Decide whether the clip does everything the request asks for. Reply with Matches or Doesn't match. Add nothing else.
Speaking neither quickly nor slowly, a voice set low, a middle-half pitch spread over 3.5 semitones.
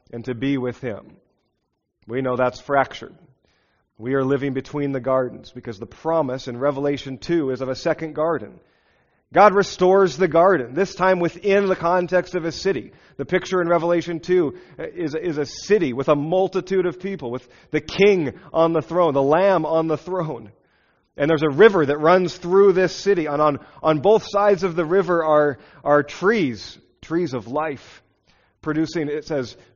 Doesn't match